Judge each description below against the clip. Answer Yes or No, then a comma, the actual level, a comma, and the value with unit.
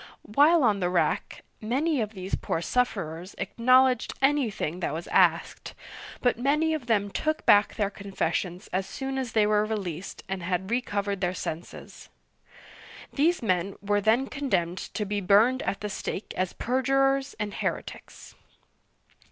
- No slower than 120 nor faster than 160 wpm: Yes, average, 150 wpm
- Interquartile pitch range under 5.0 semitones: No, wide, 5.4 semitones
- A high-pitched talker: Yes, high, 210 Hz